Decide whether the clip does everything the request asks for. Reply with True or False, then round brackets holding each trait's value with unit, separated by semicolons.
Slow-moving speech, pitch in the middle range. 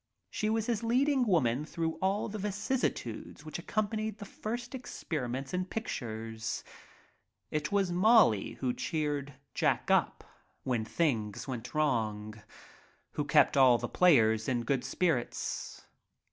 True (125 wpm; 155 Hz)